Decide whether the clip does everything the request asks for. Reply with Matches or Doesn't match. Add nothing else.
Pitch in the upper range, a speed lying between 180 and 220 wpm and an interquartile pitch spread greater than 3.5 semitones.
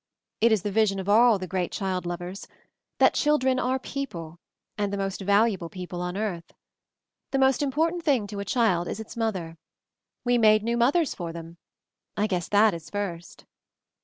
Matches